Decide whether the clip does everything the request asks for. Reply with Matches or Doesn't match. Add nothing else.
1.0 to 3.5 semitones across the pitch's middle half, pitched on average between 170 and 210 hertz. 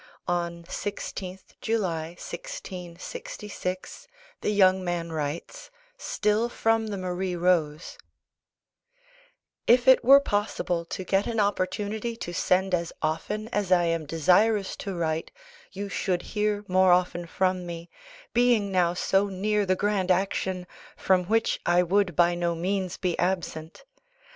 Matches